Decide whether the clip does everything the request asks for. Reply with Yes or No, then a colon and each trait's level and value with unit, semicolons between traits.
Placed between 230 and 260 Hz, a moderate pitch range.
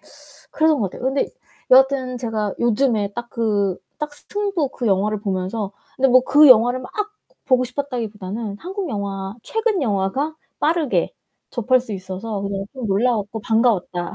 Yes: high, 235 Hz; average, 5.0 semitones